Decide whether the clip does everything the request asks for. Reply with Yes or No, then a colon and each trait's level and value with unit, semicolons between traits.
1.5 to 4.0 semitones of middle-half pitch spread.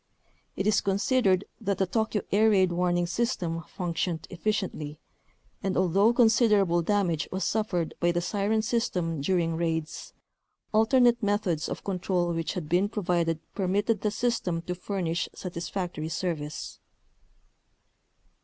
Yes: average, 3.5 semitones